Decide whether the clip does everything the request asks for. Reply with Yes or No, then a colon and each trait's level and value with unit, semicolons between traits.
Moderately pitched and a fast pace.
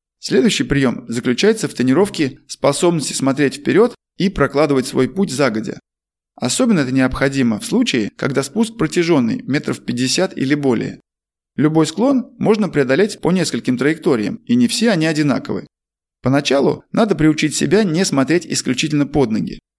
No: medium, 155 Hz; average, 140 wpm